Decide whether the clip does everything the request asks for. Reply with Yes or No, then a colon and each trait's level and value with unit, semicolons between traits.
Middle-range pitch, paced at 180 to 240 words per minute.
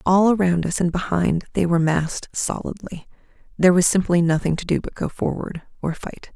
No: medium, 175 Hz; average, 170 wpm